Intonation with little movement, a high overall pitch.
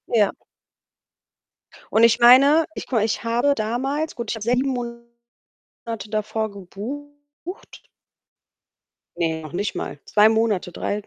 No: average, 3.9 semitones; high, 235 Hz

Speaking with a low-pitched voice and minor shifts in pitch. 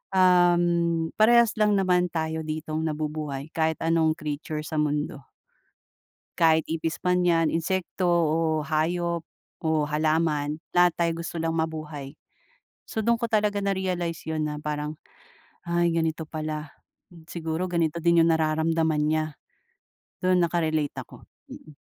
No: medium, 160 Hz; narrow, 2.0 semitones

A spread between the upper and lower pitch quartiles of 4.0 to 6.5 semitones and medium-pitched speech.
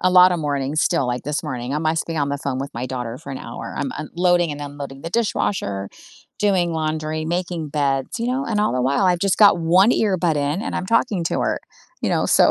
Yes: average, 4.5 semitones; medium, 155 Hz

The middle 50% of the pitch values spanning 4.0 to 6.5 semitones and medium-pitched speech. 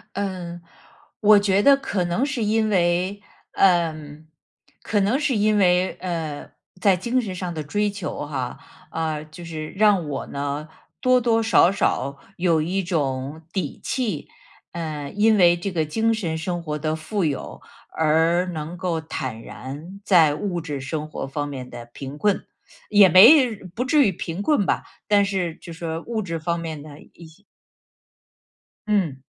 Yes: average, 4.6 semitones; medium, 175 Hz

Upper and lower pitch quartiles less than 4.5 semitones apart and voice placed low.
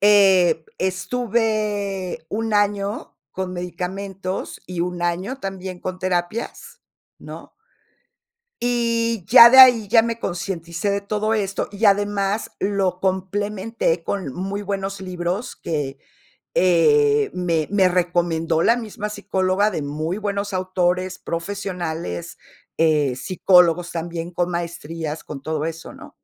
No: average, 2.9 semitones; medium, 185 Hz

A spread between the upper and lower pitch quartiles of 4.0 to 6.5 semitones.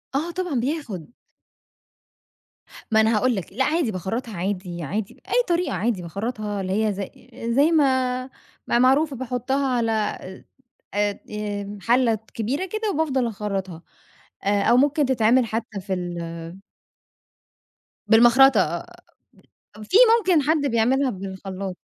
Yes: average, 5.3 semitones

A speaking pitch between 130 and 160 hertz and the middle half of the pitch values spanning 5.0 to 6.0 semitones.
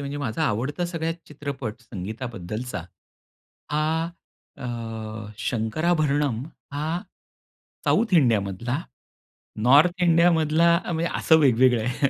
Yes: medium, 140 Hz; wide, 5.5 semitones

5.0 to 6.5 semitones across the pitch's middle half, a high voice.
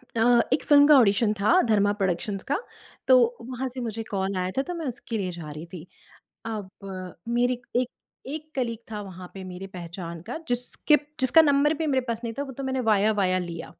Yes: wide, 5.5 semitones; high, 225 Hz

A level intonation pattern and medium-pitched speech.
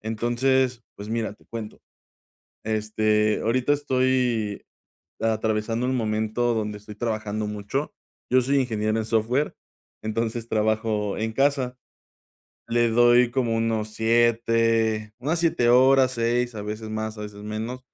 No: narrow, 2.2 semitones; low, 115 Hz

